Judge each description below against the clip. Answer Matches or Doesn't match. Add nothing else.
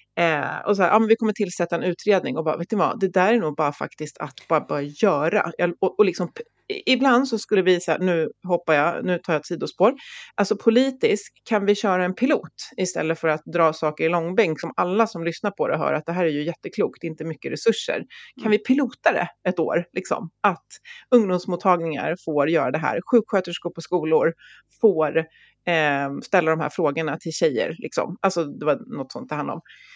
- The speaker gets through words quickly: Matches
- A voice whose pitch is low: Doesn't match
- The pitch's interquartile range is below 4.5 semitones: Doesn't match